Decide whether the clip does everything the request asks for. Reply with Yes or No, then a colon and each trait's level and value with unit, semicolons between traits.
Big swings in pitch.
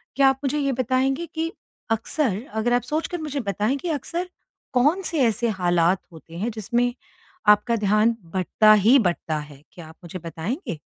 Yes: wide, 6.2 semitones